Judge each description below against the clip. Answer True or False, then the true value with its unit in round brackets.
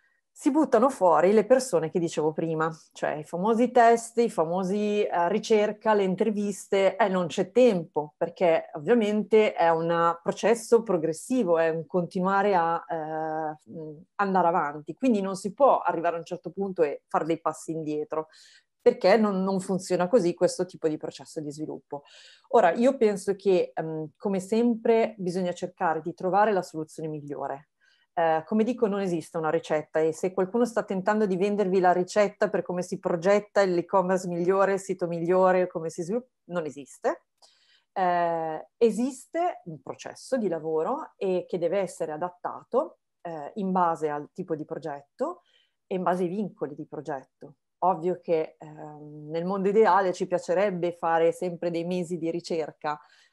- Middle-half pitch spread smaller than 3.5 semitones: False (4.0 semitones)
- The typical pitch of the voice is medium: True (180 Hz)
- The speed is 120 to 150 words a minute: False (160 wpm)